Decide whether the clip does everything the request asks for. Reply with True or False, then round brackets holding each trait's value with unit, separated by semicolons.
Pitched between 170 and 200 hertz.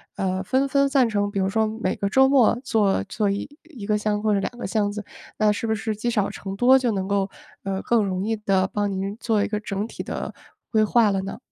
False (210 Hz)